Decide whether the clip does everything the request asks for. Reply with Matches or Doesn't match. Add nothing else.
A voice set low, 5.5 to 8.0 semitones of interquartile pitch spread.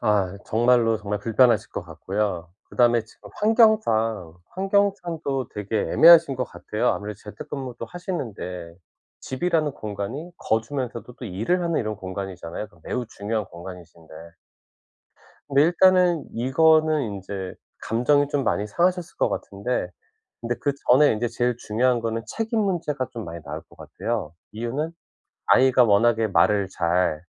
Matches